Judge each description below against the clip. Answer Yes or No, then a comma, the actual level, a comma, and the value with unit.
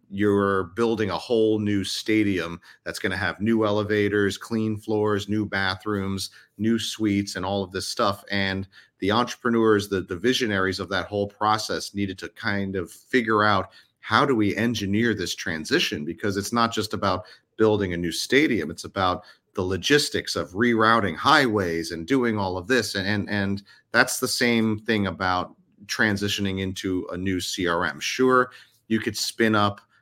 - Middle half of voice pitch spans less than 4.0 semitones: Yes, narrow, 2.4 semitones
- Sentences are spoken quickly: No, average, 170 wpm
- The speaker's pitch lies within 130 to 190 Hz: No, low, 105 Hz